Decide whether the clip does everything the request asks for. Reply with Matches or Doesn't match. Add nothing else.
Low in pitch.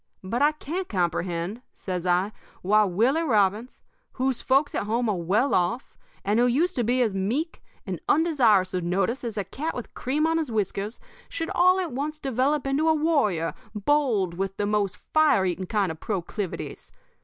Doesn't match